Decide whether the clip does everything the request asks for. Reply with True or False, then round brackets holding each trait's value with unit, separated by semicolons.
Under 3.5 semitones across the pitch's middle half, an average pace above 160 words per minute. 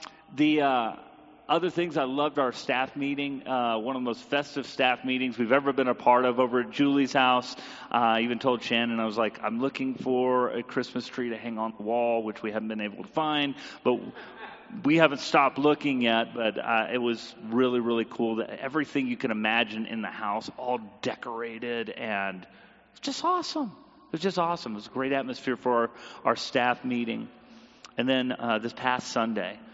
True (3.0 semitones; 200 wpm)